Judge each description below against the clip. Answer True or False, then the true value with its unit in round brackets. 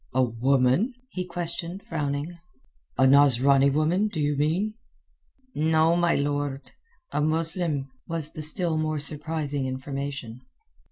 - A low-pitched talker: False (150 Hz)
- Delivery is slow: True (120 wpm)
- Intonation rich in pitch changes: False (3.1 semitones)